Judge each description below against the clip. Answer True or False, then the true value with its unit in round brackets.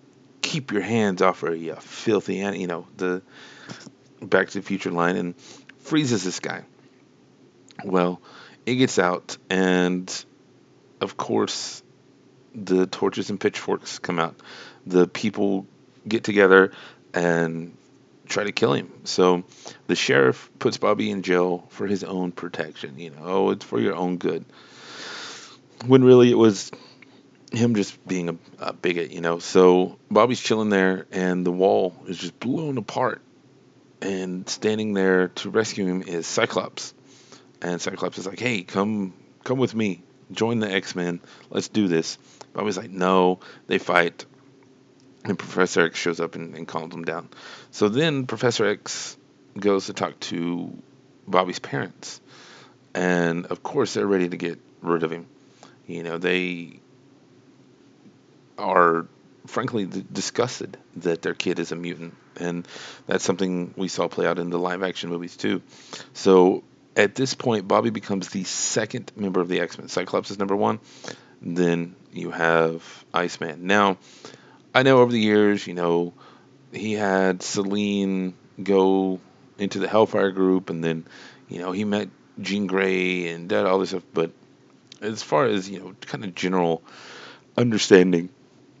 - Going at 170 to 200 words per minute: False (150 wpm)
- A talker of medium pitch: False (95 Hz)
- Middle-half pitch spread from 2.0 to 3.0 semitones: True (2.7 semitones)